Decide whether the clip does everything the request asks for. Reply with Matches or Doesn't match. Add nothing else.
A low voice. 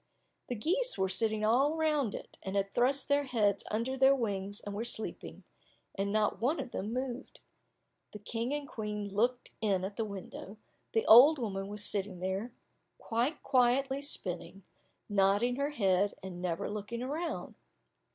Doesn't match